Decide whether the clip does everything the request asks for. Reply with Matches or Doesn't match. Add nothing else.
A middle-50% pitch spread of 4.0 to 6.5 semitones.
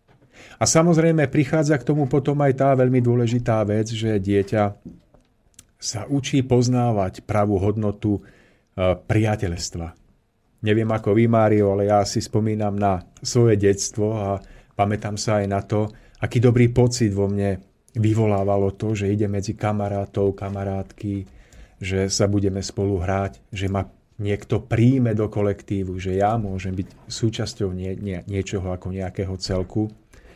Doesn't match